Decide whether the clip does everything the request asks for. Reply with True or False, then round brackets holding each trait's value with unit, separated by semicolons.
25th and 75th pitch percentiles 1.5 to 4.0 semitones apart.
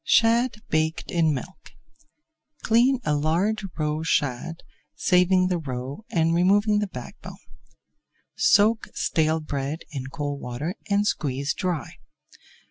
False (5.6 semitones)